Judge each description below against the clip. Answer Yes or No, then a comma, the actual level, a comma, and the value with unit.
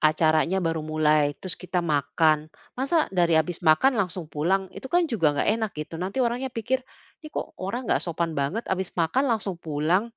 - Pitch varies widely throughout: Yes, wide, 6.3 semitones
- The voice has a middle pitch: Yes, medium, 175 Hz